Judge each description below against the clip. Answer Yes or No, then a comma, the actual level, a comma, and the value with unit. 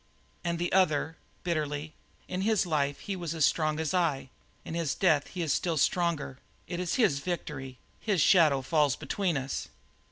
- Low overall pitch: No, medium, 160 Hz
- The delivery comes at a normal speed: Yes, average, 170 wpm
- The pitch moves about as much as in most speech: Yes, average, 3.5 semitones